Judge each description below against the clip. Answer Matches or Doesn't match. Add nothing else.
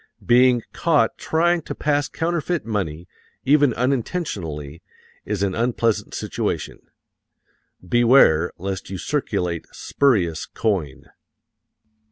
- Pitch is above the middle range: Doesn't match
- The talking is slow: Matches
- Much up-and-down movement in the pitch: Matches